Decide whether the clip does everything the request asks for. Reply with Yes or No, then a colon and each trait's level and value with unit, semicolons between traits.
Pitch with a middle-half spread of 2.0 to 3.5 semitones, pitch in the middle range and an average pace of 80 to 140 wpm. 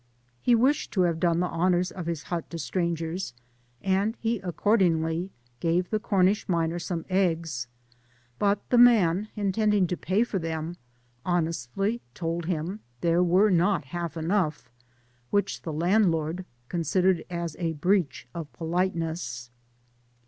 Yes: average, 2.9 semitones; medium, 175 Hz; slow, 135 wpm